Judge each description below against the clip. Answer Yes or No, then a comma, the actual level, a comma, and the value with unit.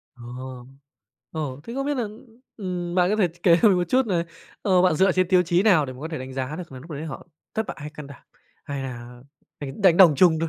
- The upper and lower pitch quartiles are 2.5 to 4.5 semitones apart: No, average, 5.2 semitones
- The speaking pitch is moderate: Yes, medium, 165 Hz